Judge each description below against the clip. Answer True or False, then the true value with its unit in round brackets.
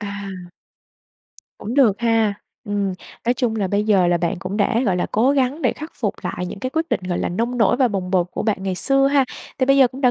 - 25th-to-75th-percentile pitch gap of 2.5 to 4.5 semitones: False (4.9 semitones)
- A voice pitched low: False (220 Hz)